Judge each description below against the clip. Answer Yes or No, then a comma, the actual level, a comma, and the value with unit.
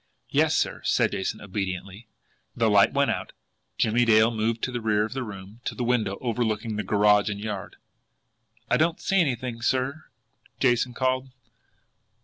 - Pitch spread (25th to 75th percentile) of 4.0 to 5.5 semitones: No, average, 3.4 semitones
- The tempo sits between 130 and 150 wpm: No, average, 160 wpm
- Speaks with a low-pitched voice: Yes, low, 115 Hz